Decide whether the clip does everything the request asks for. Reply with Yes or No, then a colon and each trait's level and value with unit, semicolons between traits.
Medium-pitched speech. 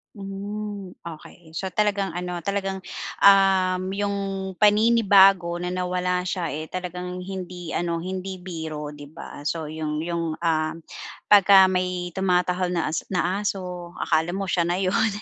Yes: medium, 180 Hz